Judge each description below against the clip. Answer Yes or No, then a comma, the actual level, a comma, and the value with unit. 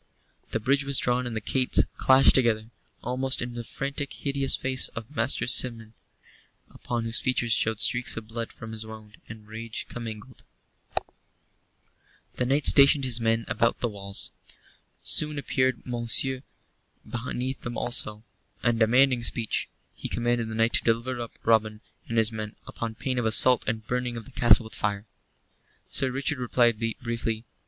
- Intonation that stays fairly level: Yes, narrow, 2.3 semitones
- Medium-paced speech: Yes, average, 160 wpm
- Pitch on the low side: Yes, low, 120 Hz